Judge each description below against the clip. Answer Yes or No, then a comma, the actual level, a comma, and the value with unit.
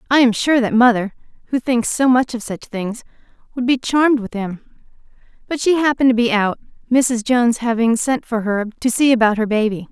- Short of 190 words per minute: No, fast, 205 wpm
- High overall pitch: Yes, high, 235 Hz